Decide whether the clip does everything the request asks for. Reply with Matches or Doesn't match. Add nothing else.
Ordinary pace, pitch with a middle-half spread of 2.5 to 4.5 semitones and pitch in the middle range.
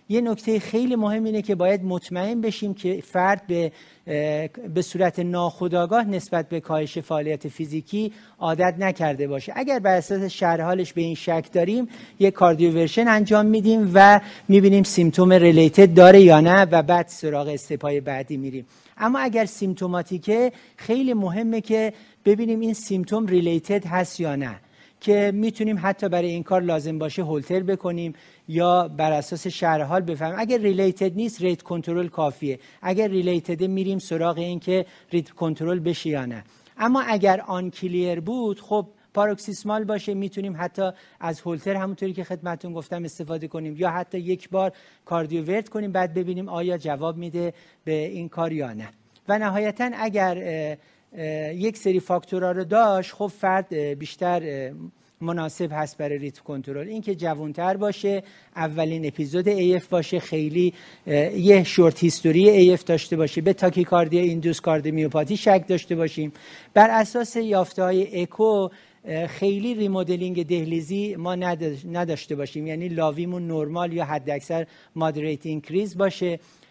Matches